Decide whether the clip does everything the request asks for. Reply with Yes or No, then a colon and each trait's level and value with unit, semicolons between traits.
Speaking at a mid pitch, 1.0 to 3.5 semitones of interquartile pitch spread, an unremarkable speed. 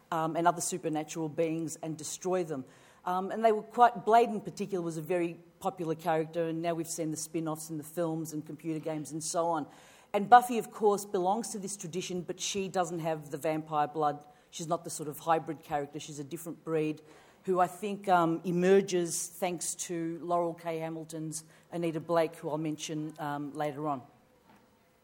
Yes: medium, 165 Hz; narrow, 2.5 semitones; average, 195 wpm